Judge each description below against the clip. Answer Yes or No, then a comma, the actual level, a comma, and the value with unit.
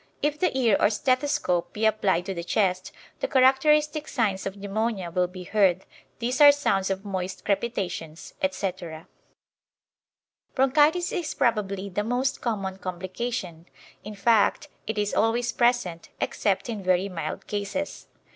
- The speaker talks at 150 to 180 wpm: No, average, 140 wpm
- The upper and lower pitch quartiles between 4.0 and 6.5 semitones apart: Yes, average, 4.8 semitones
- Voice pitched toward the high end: Yes, high, 205 Hz